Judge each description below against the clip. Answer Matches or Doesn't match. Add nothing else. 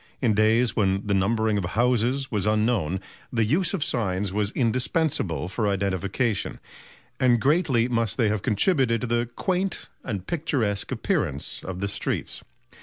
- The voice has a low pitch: Matches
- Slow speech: Doesn't match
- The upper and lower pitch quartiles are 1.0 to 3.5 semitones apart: Doesn't match